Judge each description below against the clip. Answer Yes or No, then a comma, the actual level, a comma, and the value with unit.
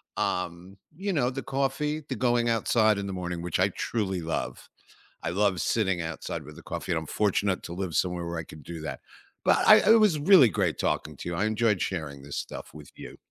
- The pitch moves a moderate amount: No, wide, 5.7 semitones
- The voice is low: Yes, very low, 95 Hz